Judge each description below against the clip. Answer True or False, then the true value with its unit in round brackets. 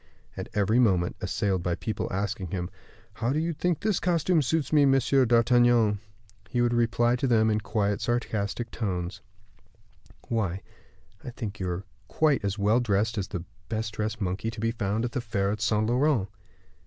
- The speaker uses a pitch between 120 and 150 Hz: False (110 Hz)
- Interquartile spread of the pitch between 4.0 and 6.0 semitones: False (3.4 semitones)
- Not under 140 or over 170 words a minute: False (180 wpm)